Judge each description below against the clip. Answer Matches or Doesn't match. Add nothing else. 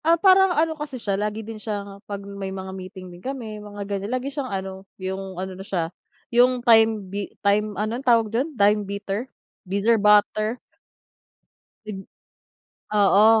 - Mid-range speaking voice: Doesn't match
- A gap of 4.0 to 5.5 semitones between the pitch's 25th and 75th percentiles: Doesn't match